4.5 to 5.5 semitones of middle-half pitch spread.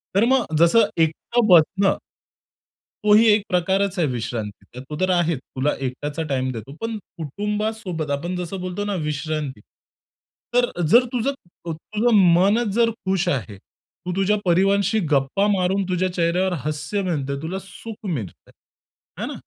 Yes: average, 5.2 semitones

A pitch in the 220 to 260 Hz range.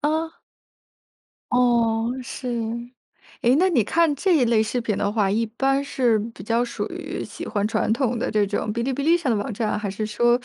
Yes: high, 235 Hz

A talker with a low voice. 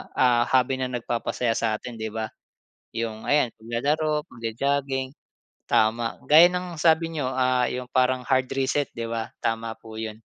Yes: low, 125 Hz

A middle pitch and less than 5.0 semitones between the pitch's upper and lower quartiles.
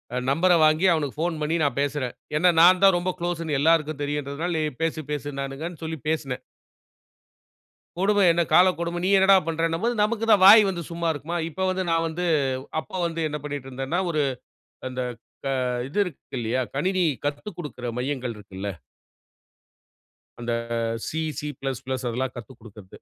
Yes: medium, 155 Hz; average, 4.3 semitones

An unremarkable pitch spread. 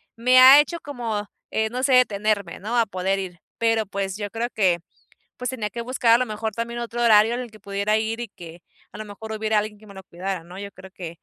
Yes: average, 3.0 semitones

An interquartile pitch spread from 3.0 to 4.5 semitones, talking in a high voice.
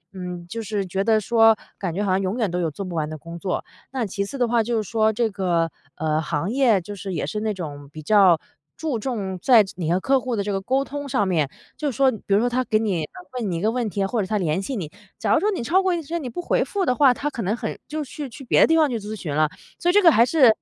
No: wide, 5.6 semitones; high, 215 Hz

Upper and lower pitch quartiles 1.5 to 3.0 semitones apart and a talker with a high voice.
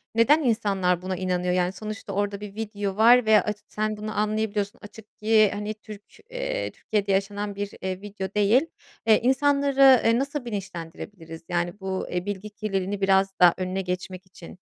Yes: narrow, 2.5 semitones; high, 205 Hz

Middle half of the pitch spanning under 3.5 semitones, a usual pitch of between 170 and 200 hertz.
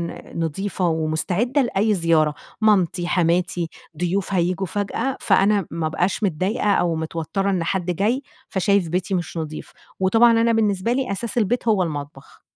No: average, 3.8 semitones; high, 190 Hz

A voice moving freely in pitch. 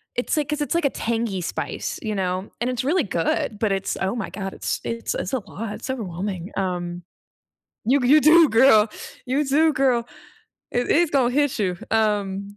Yes: wide, 5.7 semitones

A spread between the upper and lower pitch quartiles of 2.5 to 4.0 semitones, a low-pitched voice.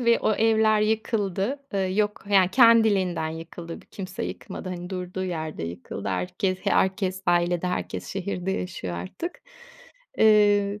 No: average, 3.3 semitones; high, 190 Hz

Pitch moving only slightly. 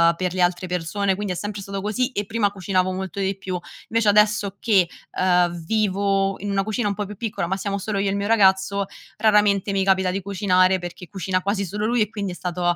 Yes: narrow, 1.9 semitones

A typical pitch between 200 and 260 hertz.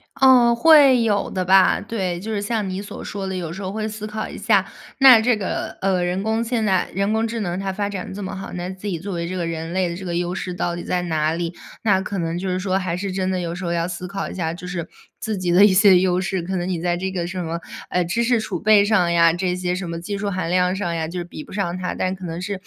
No: medium, 185 Hz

